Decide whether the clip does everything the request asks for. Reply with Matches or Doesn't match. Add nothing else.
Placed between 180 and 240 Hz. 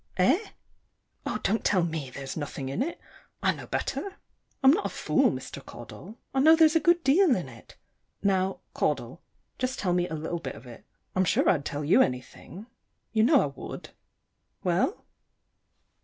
Matches